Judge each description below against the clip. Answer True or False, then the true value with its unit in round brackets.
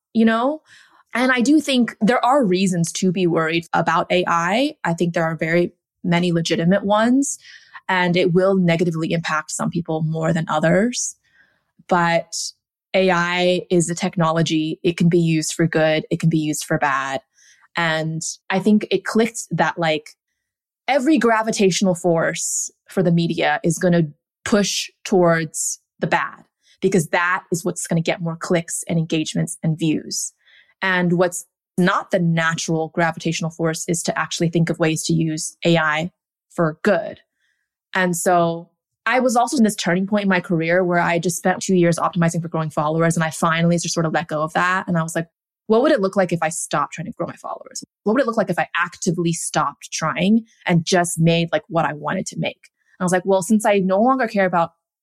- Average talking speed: True (195 wpm)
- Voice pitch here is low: False (175 Hz)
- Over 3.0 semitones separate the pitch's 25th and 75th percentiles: False (2.6 semitones)